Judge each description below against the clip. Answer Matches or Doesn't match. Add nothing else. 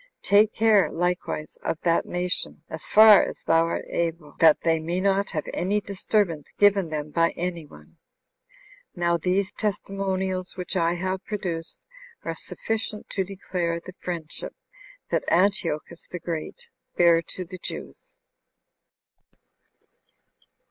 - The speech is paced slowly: Matches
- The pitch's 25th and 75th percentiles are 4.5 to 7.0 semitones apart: Doesn't match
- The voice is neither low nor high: Matches